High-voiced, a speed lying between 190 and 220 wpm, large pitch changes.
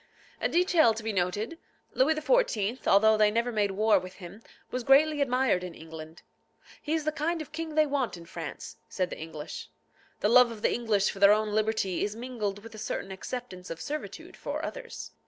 Yes: high, 220 Hz; average, 195 wpm; wide, 6.0 semitones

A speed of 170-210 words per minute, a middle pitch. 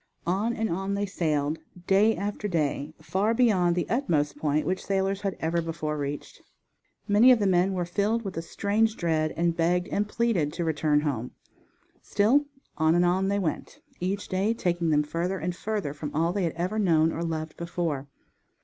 Yes: average, 185 wpm; medium, 175 Hz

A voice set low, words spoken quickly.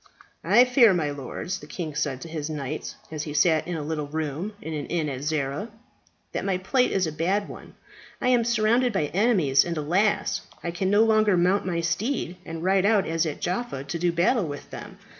No: medium, 170 Hz; fast, 215 wpm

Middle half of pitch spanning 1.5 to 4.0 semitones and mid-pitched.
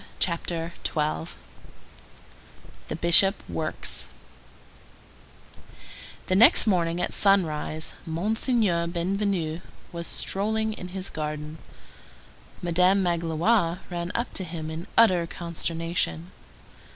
Yes: average, 2.9 semitones; medium, 170 Hz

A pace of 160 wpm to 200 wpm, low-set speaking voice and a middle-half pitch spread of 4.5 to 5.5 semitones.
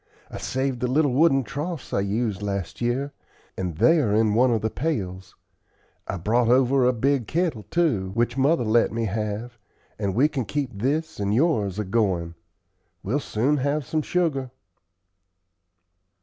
Yes: average, 165 wpm; low, 120 Hz; average, 5.2 semitones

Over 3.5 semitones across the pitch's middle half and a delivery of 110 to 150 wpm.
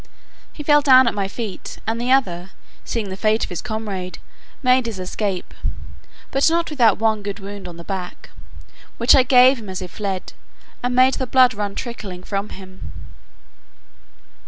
No: average, 4.7 semitones; average, 175 wpm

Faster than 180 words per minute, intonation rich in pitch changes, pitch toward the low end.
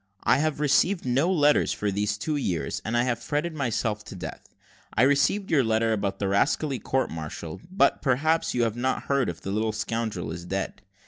Yes: average, 200 wpm; wide, 5.8 semitones; low, 120 Hz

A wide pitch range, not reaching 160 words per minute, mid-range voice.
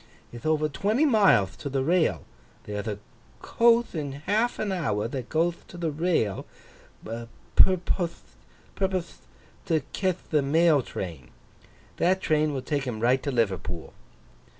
Yes: wide, 7.2 semitones; slow, 135 wpm; medium, 155 Hz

